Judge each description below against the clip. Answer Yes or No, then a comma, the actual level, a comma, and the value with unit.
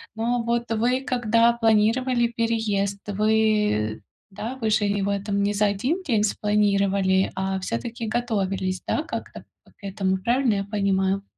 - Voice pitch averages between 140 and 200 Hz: No, high, 210 Hz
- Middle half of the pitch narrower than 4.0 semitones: Yes, average, 2.8 semitones